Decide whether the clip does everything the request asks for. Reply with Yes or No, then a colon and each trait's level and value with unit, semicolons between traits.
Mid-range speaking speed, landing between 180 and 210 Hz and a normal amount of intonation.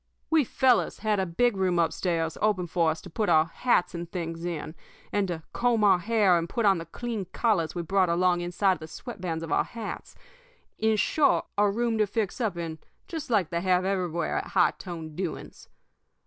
No: fast, 210 wpm; medium, 185 Hz; average, 4.1 semitones